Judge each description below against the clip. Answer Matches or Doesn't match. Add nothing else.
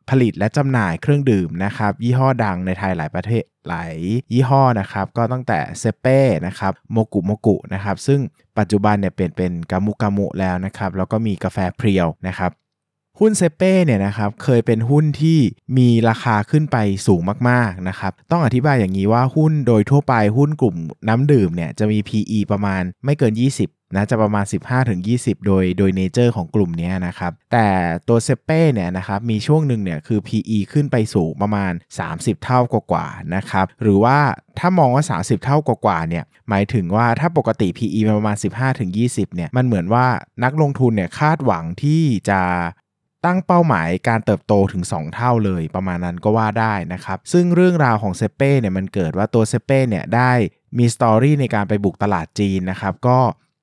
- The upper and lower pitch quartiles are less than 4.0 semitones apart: Doesn't match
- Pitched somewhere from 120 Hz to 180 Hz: Doesn't match